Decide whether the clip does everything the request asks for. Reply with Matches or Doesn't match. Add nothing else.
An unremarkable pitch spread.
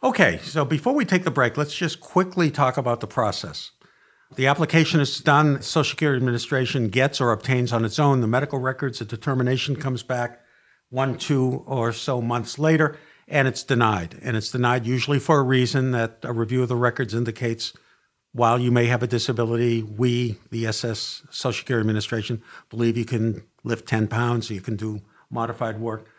Matches